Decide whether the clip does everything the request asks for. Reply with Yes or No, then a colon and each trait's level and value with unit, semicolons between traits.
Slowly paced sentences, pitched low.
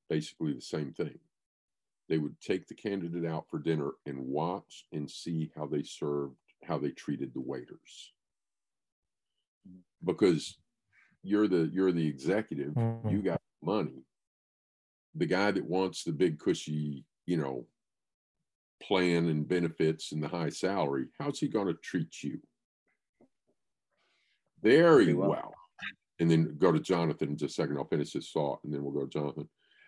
No: average, 150 wpm; very low, 80 Hz